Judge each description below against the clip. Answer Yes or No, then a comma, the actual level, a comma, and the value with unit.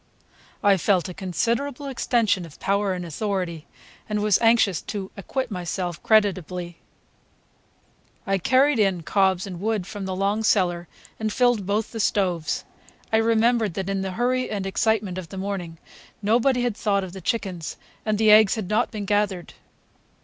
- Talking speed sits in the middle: Yes, average, 165 wpm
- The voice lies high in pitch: Yes, high, 200 Hz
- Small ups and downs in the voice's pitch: No, average, 3.2 semitones